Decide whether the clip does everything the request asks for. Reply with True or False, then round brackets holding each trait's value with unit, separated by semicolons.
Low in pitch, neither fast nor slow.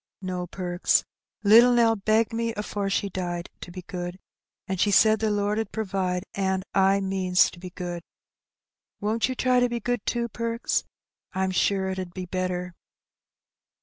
False (195 Hz; 170 wpm)